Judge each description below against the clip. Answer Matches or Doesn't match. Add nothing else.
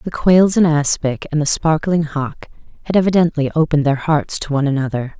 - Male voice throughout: Doesn't match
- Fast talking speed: Doesn't match